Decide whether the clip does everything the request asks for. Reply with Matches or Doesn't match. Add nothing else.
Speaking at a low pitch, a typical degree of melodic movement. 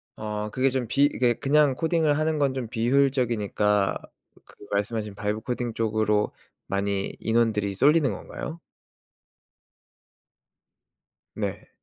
Matches